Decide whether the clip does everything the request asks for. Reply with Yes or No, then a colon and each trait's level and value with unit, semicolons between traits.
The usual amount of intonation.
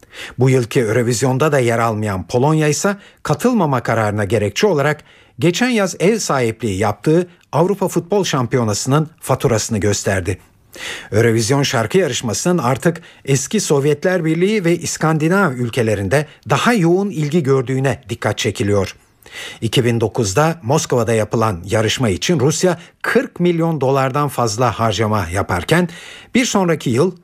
No: wide, 6.7 semitones